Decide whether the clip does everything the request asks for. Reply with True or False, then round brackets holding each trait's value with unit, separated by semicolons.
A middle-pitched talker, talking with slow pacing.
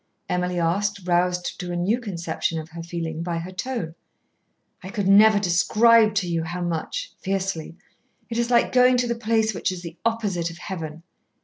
False (180 Hz; 185 wpm)